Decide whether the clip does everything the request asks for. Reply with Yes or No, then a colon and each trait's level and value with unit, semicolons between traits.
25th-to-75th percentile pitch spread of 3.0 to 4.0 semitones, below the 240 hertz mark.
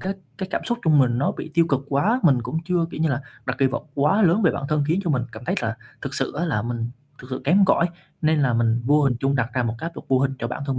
No: average, 5.0 semitones; medium, 140 Hz